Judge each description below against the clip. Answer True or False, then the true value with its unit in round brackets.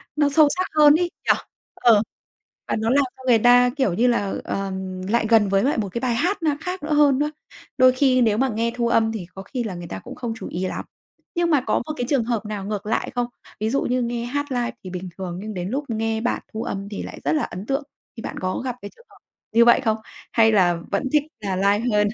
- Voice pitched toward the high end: True (235 Hz)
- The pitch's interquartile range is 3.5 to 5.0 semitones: True (4.3 semitones)